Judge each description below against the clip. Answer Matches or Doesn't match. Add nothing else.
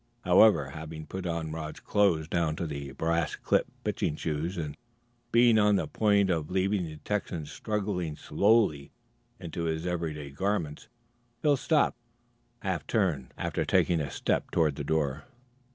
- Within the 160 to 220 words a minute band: Doesn't match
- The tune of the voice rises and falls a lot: Doesn't match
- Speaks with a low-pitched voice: Matches